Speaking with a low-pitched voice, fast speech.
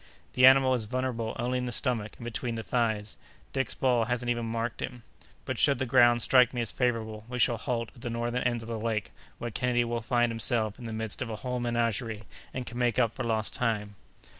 Yes: low, 120 Hz; fast, 230 wpm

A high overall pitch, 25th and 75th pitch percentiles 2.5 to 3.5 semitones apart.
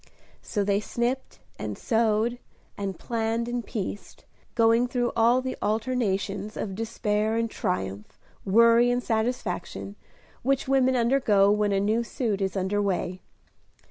Yes: high, 220 Hz; average, 3.1 semitones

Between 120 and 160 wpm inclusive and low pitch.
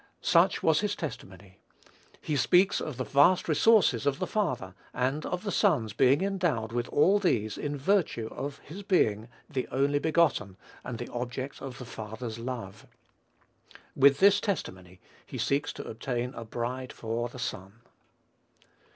Yes: average, 155 wpm; low, 130 Hz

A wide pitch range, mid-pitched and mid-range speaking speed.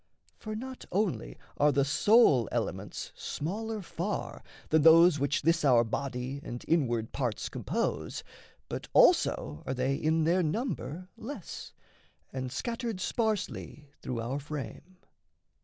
No: wide, 7.1 semitones; medium, 155 Hz; slow, 125 wpm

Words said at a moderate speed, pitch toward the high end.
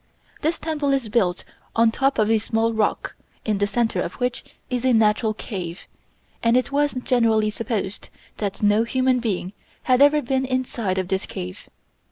Yes: average, 175 wpm; high, 230 Hz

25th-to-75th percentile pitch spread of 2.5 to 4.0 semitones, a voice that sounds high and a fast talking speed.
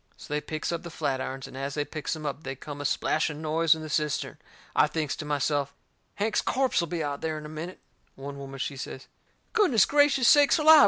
No: average, 3.2 semitones; medium, 155 Hz; fast, 225 wpm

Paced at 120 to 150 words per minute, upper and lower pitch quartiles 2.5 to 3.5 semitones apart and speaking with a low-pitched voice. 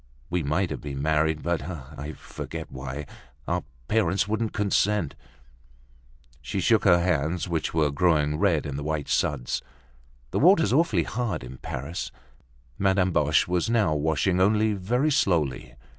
No: average, 140 wpm; average, 5.1 semitones; very low, 85 Hz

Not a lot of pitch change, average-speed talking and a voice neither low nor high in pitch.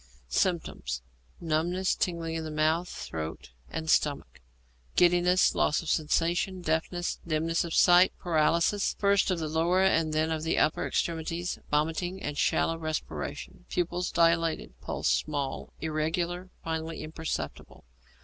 No: narrow, 2.1 semitones; slow, 130 wpm; medium, 165 Hz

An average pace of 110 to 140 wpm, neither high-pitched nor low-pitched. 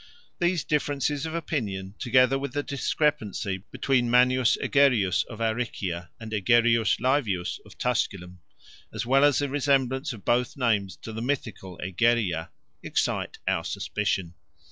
No: slow, 135 wpm; low, 120 Hz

